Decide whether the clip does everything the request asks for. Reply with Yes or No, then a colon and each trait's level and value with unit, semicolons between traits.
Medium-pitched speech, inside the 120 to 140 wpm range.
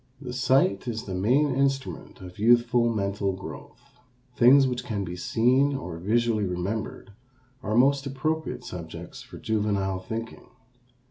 No: low, 115 Hz; slow, 135 wpm